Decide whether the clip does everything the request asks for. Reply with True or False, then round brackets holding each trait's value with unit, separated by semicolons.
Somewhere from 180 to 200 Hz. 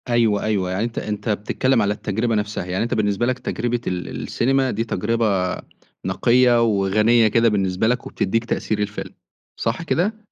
False (110 Hz)